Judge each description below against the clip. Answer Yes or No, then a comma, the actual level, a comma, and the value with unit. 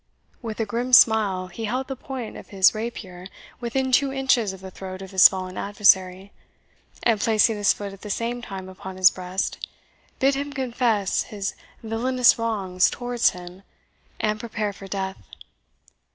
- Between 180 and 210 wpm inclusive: No, average, 165 wpm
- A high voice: Yes, high, 210 Hz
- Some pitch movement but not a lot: Yes, average, 3.9 semitones